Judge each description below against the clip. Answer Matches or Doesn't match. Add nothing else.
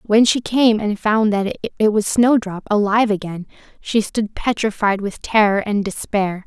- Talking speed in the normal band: Matches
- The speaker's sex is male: Doesn't match